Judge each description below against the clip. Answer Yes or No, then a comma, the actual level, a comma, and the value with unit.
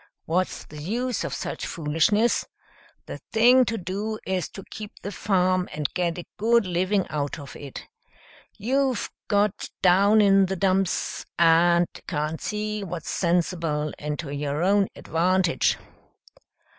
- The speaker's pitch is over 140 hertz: Yes, medium, 185 Hz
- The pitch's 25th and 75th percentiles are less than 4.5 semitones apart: Yes, average, 4.0 semitones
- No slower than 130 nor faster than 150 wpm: Yes, average, 140 wpm